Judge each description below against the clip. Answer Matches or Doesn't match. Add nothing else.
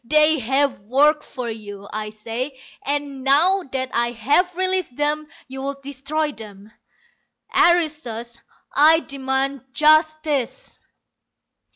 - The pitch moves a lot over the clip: Doesn't match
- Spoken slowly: Matches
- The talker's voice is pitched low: Doesn't match